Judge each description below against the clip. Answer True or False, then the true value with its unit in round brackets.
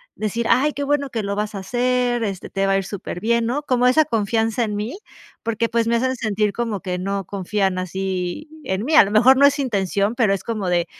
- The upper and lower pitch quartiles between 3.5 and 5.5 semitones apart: True (3.8 semitones)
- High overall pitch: True (220 Hz)